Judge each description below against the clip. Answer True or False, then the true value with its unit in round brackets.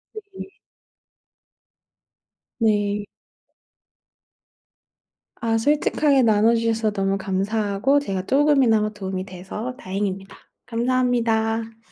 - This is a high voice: True (220 Hz)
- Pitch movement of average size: True (3.7 semitones)